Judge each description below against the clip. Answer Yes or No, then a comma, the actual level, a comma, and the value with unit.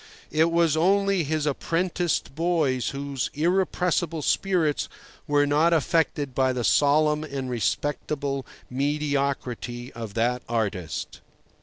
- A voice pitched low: No, medium, 145 Hz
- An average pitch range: Yes, average, 3.9 semitones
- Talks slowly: Yes, slow, 110 wpm